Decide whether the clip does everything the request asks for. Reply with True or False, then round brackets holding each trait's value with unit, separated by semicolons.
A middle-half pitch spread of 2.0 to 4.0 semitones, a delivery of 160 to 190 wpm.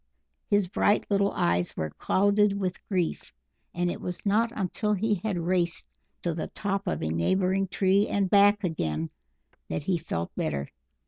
True (3.3 semitones; 165 wpm)